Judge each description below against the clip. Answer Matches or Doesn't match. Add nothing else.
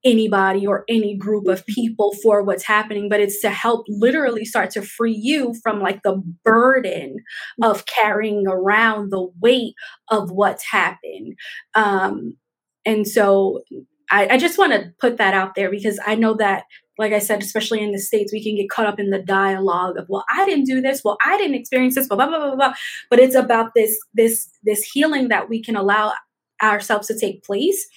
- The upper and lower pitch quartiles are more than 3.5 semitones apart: Doesn't match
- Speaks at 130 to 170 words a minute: Doesn't match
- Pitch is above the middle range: Matches